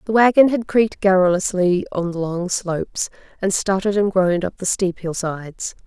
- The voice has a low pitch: No, high, 190 Hz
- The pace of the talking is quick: No, average, 185 wpm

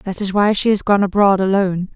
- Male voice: No, female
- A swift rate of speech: Yes, fast, 245 wpm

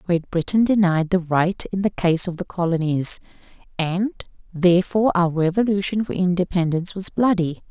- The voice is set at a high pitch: No, medium, 180 Hz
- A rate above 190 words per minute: No, average, 150 wpm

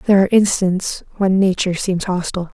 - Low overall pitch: No, high, 190 Hz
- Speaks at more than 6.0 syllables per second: Yes, 6.3 syllables/s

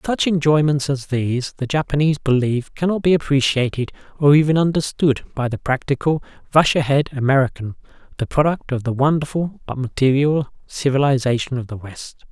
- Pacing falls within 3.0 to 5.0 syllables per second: No, 5.7 syllables/s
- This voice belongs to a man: Yes, male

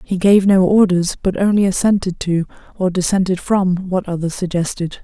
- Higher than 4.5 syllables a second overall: Yes, 5.0 syllables/s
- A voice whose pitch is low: No, medium, 185 Hz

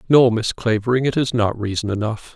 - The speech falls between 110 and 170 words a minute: No, fast, 205 wpm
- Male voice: Yes, male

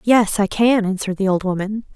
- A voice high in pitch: Yes, high, 205 Hz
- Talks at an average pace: No, fast, 215 wpm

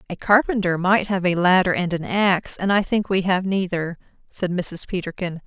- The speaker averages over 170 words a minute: Yes, average, 200 wpm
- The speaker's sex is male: No, female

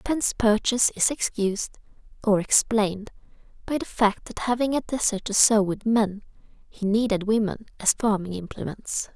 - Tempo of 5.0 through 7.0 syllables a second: No, 4.8 syllables/s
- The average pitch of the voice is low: No, high, 215 Hz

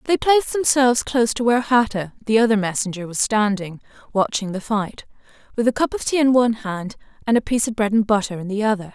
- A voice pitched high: Yes, high, 220 Hz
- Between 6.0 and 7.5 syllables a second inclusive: Yes, 6.3 syllables/s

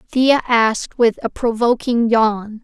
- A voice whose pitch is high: Yes, high, 230 Hz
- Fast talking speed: No, slow, 135 wpm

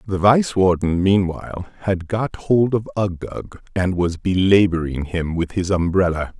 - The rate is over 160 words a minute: No, average, 150 wpm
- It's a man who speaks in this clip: Yes, male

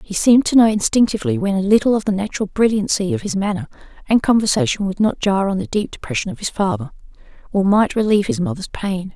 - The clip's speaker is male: No, female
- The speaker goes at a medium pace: No, fast, 215 wpm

